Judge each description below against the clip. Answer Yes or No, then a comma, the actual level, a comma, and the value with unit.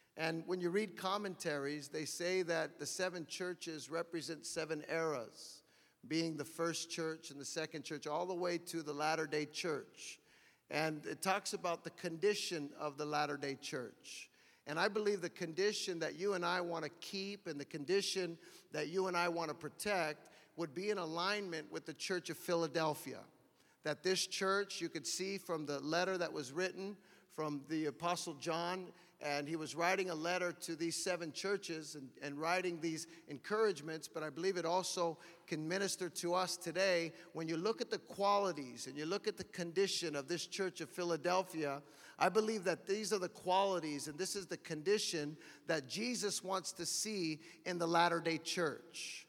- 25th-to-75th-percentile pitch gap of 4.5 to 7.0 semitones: No, average, 2.9 semitones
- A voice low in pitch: No, medium, 170 Hz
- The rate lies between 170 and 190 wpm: Yes, average, 185 wpm